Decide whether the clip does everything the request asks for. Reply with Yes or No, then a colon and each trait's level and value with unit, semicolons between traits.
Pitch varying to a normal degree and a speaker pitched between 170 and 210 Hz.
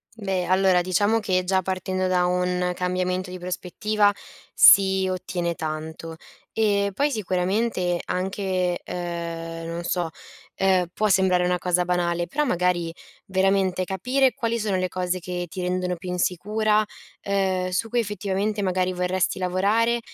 No: narrow, 1.8 semitones; medium, 185 Hz